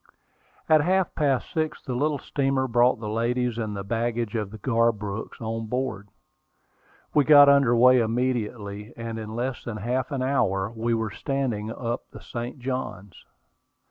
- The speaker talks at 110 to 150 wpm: No, average, 160 wpm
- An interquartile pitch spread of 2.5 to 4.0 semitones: Yes, average, 3.1 semitones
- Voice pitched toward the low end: Yes, low, 120 Hz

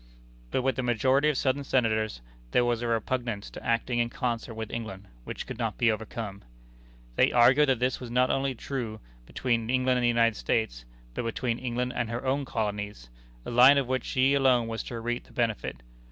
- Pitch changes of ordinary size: No, narrow, 2.3 semitones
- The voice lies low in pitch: Yes, low, 120 Hz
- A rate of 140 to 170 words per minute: No, fast, 205 wpm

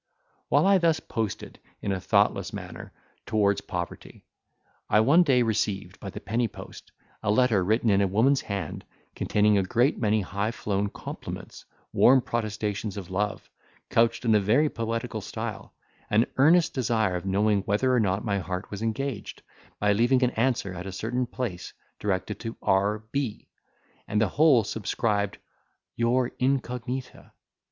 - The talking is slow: No, average, 155 wpm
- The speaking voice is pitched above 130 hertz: No, low, 110 Hz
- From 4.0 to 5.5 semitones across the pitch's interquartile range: No, average, 3.6 semitones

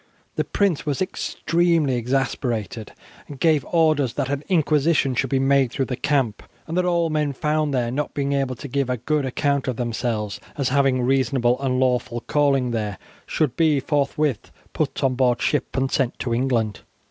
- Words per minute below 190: Yes, average, 180 wpm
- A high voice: No, low, 135 Hz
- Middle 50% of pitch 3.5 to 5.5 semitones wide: No, average, 2.9 semitones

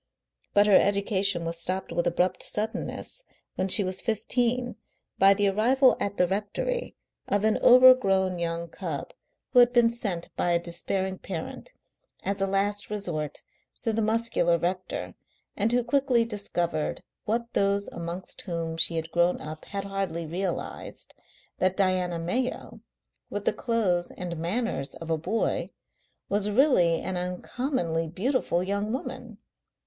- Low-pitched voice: No, high, 195 Hz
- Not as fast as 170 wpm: Yes, average, 145 wpm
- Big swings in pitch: No, average, 4.6 semitones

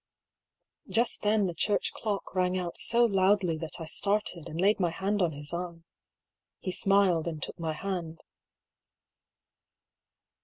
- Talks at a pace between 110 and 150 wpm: Yes, average, 145 wpm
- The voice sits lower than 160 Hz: No, medium, 185 Hz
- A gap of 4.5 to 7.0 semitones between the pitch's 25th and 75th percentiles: No, average, 3.2 semitones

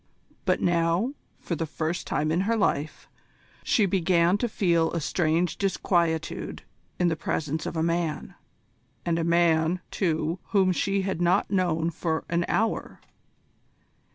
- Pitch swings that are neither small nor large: No, narrow, 2.2 semitones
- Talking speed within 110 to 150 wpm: Yes, average, 145 wpm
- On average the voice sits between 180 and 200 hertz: No, medium, 170 Hz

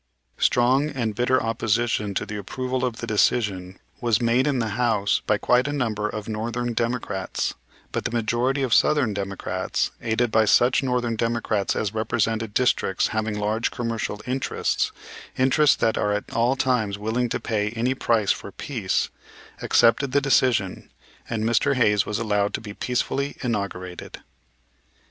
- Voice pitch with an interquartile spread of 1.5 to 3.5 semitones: Yes, average, 2.9 semitones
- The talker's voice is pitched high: No, low, 115 Hz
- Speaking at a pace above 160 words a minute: No, average, 155 wpm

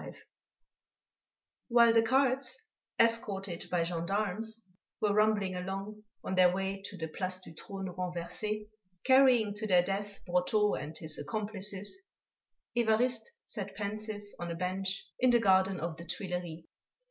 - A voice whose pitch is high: Yes, high, 195 Hz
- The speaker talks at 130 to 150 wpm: Yes, slow, 135 wpm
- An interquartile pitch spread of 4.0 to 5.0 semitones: No, average, 3.1 semitones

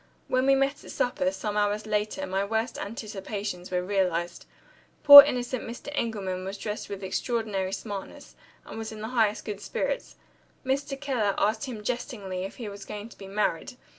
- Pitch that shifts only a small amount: No, average, 3.8 semitones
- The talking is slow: No, average, 175 wpm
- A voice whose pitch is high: Yes, high, 210 Hz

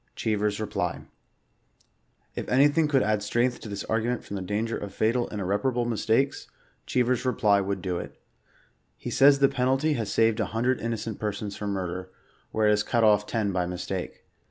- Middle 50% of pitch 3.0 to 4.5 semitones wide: Yes, average, 3.3 semitones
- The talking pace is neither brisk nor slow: Yes, average, 175 wpm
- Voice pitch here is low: Yes, low, 110 Hz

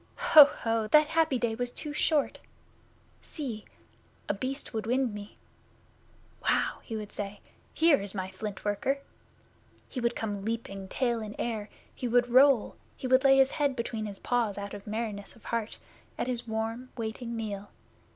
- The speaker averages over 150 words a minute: Yes, average, 170 wpm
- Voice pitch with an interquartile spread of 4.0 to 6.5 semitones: No, average, 3.6 semitones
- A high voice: Yes, high, 230 Hz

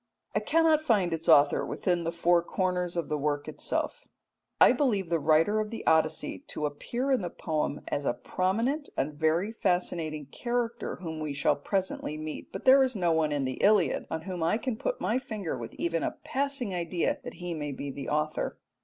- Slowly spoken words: No, average, 200 wpm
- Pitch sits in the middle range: Yes, medium, 175 Hz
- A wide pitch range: Yes, wide, 5.9 semitones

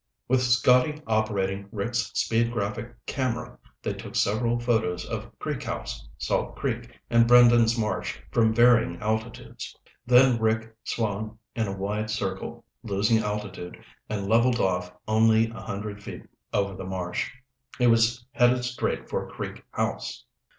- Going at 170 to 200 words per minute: No, average, 140 wpm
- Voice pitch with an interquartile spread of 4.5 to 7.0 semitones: No, average, 2.7 semitones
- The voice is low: Yes, low, 110 Hz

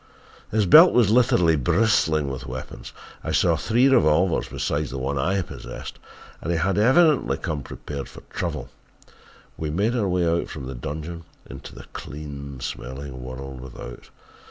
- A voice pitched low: Yes, very low, 80 Hz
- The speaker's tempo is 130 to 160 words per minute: Yes, average, 155 wpm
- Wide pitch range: Yes, wide, 6.4 semitones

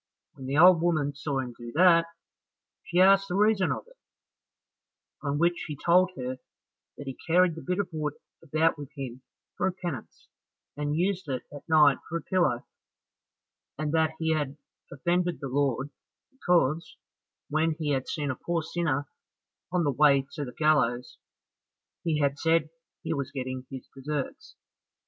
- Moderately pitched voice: Yes, medium, 155 Hz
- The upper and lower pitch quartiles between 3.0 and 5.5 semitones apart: Yes, average, 3.8 semitones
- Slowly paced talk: No, average, 165 wpm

